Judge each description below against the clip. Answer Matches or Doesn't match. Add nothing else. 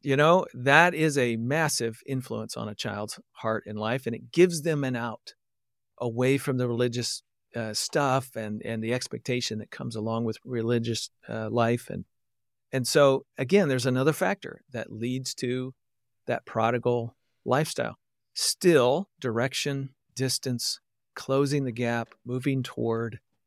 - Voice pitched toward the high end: Doesn't match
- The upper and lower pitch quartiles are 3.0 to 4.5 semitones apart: Doesn't match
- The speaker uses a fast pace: Doesn't match